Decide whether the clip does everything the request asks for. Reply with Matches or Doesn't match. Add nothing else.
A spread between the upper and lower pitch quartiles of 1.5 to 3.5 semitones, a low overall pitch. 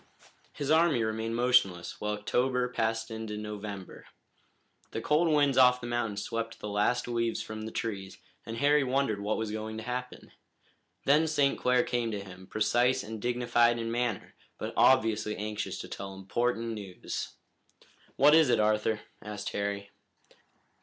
Matches